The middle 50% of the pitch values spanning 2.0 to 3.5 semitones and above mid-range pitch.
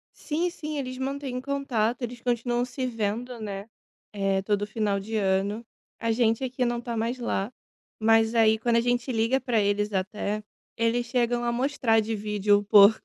Yes: average, 2.8 semitones; high, 230 Hz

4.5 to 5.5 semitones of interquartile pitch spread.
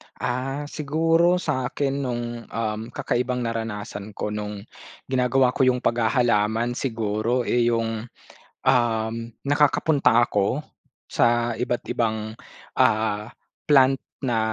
No: average, 2.9 semitones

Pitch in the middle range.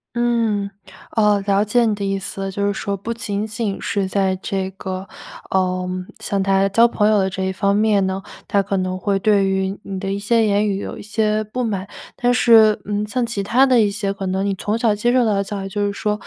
No: high, 200 Hz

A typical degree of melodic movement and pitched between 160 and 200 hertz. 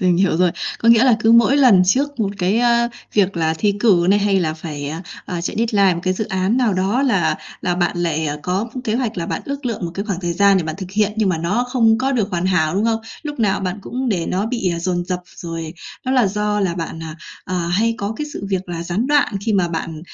Yes: average, 4.5 semitones; high, 195 Hz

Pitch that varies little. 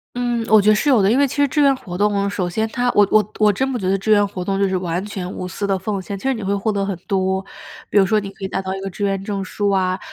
Yes: narrow, 2.2 semitones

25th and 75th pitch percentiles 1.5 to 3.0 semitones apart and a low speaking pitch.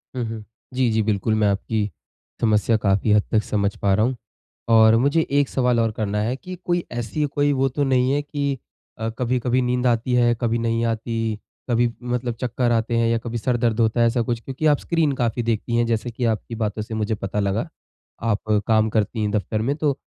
Yes: narrow, 2.4 semitones; low, 115 Hz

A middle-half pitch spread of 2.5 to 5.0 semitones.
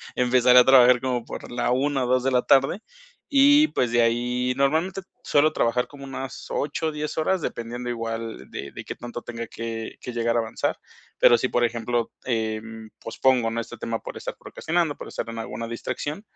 Yes: average, 2.8 semitones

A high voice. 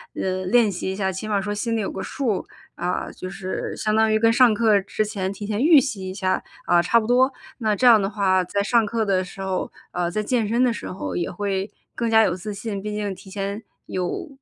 Yes: high, 205 Hz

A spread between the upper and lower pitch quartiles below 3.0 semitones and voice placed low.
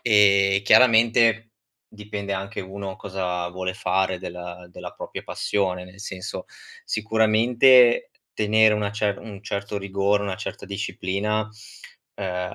Yes: narrow, 2.4 semitones; low, 100 Hz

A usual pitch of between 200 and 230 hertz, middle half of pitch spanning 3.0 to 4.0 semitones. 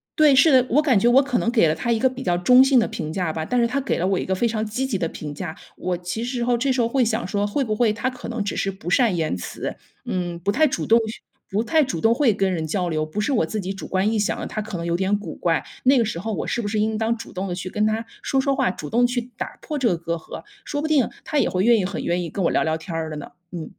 No: high, 215 Hz; wide, 5.5 semitones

